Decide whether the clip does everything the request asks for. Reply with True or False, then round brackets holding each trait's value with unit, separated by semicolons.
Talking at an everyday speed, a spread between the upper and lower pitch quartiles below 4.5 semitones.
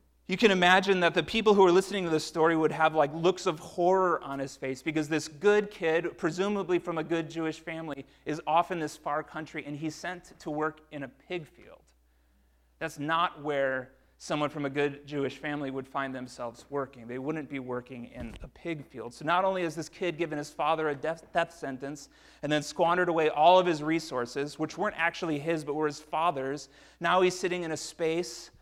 False (215 wpm; 3.3 semitones)